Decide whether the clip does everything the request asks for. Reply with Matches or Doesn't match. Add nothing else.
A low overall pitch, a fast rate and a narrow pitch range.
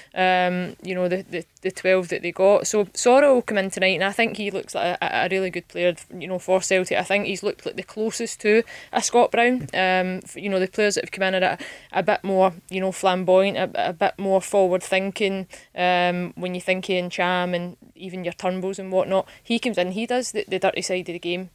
Doesn't match